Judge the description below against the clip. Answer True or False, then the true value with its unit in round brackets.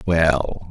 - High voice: False (85 Hz)